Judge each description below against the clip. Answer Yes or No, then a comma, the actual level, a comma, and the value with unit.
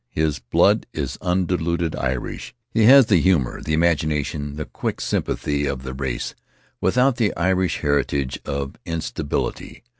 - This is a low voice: Yes, very low, 75 Hz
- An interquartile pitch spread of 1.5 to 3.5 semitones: No, average, 4.4 semitones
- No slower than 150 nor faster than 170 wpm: No, average, 140 wpm